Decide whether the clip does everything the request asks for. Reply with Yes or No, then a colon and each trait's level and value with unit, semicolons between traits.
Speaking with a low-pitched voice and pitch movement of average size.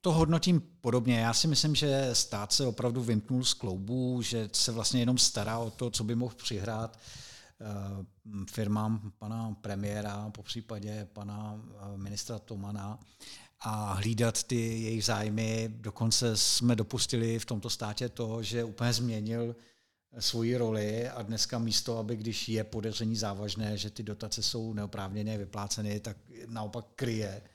No: low, 115 Hz; narrow, 2.1 semitones